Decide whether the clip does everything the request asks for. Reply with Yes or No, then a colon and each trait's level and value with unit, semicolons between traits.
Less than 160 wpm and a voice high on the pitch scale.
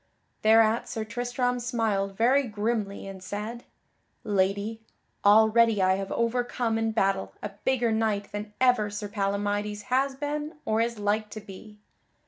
Yes: average, 140 wpm; high, 220 Hz